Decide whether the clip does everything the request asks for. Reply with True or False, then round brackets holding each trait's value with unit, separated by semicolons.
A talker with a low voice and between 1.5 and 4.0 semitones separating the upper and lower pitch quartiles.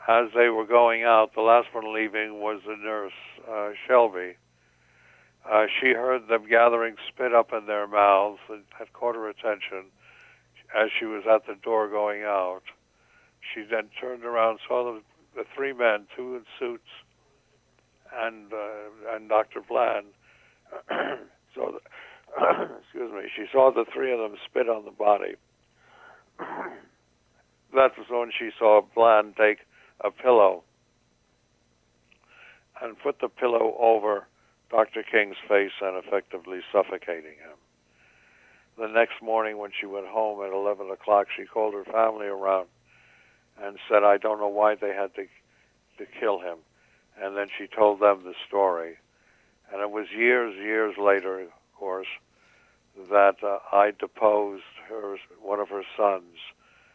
True (105 Hz; 2.8 semitones)